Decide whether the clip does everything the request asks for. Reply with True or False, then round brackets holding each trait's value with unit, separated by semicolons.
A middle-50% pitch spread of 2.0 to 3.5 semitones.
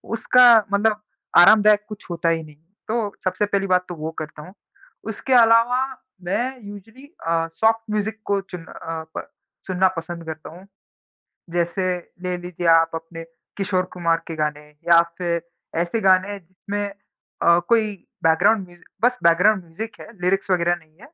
False (4.0 semitones)